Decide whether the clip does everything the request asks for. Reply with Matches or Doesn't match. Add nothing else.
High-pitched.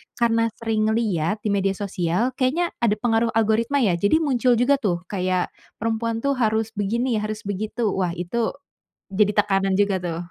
Matches